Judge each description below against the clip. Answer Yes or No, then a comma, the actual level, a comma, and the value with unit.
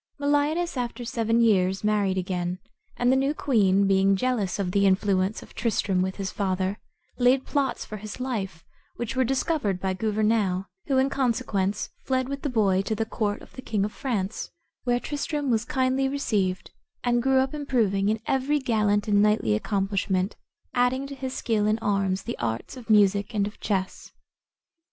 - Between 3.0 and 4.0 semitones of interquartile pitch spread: No, average, 4.8 semitones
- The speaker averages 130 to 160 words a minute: No, average, 175 wpm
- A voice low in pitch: No, high, 215 Hz